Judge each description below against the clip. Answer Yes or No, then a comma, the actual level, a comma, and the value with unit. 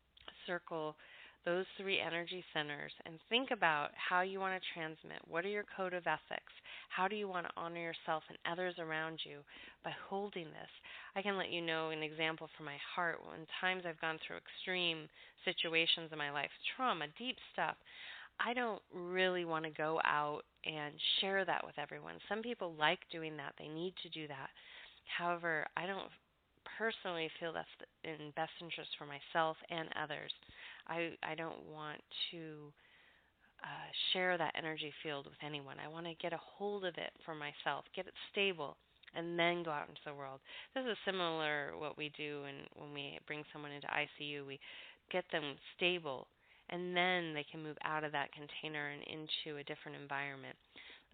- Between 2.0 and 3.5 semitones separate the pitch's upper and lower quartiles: Yes, average, 3.2 semitones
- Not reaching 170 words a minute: No, average, 180 wpm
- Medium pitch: Yes, medium, 165 Hz